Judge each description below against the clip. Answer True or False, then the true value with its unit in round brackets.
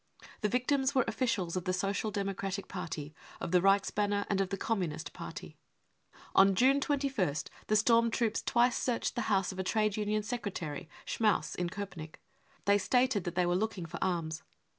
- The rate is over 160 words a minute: True (175 wpm)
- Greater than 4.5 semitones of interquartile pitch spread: False (3.8 semitones)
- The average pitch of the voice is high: True (200 Hz)